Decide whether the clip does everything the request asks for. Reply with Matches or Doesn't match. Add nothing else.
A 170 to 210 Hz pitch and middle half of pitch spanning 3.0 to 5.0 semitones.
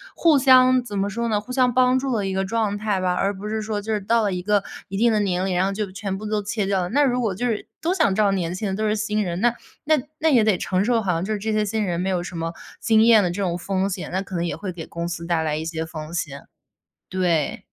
Matches